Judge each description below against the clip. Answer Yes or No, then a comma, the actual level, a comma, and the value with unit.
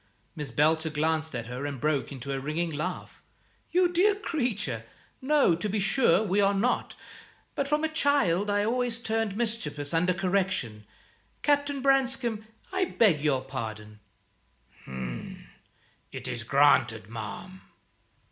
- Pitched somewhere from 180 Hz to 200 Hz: Yes, medium, 185 Hz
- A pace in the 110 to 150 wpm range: Yes, slow, 135 wpm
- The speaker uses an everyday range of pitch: No, wide, 8.8 semitones